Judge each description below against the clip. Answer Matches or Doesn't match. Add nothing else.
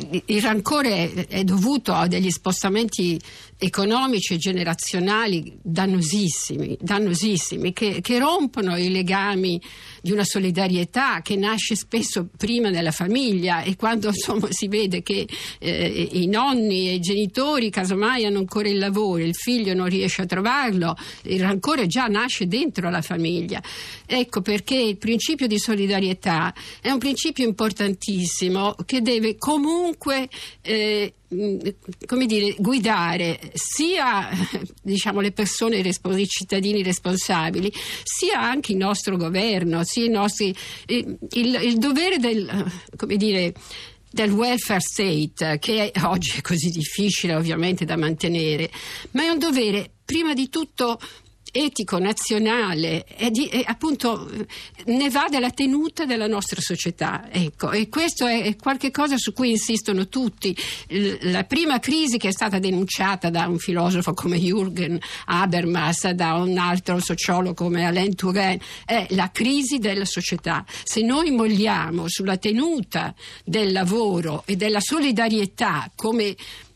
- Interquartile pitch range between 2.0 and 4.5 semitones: Matches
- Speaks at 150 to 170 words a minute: Doesn't match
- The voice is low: Doesn't match